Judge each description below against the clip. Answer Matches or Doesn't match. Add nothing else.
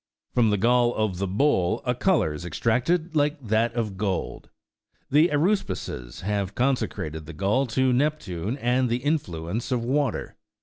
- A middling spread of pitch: Doesn't match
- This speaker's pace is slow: Doesn't match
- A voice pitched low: Matches